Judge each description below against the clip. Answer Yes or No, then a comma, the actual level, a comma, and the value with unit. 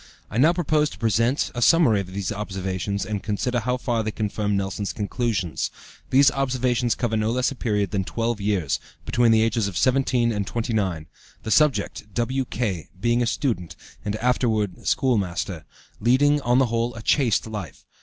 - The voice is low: Yes, low, 115 Hz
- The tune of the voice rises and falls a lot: No, average, 3.6 semitones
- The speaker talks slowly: No, average, 170 wpm